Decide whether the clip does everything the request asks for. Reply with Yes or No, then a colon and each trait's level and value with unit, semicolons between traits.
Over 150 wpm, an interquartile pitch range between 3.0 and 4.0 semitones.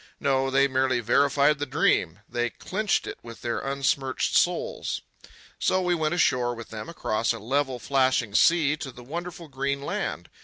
Yes: average, 165 wpm; average, 3.4 semitones